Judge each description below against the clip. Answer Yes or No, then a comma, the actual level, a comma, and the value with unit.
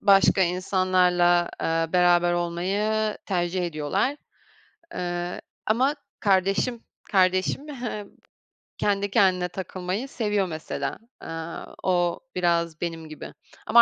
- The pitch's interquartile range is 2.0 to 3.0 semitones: Yes, narrow, 2.4 semitones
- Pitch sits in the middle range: Yes, medium, 180 Hz